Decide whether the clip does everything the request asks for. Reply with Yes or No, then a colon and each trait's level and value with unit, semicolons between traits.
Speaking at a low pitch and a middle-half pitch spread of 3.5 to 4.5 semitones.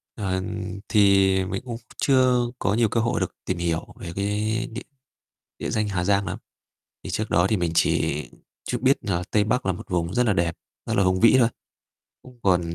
Yes: low, 100 Hz; average, 3.8 semitones